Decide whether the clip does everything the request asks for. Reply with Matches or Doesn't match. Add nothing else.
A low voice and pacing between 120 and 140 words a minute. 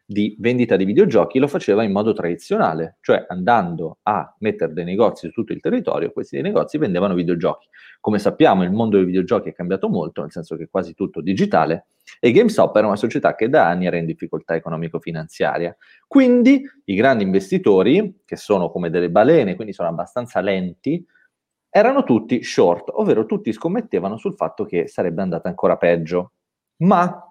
Doesn't match